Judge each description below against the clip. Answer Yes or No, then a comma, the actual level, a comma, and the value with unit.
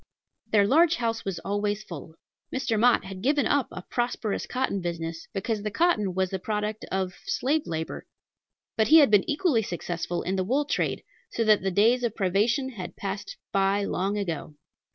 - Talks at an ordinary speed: Yes, average, 180 wpm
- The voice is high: Yes, high, 205 Hz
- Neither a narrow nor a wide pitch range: Yes, average, 4.2 semitones